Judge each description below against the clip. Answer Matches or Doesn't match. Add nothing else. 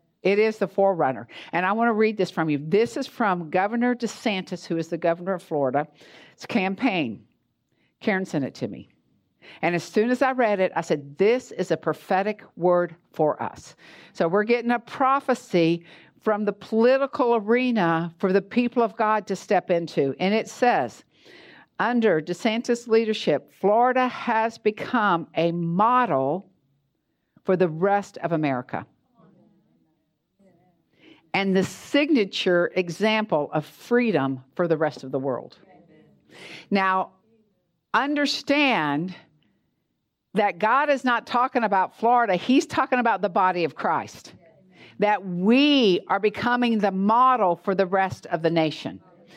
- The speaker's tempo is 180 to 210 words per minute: Doesn't match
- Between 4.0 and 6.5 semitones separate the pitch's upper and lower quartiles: Matches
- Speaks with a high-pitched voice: Matches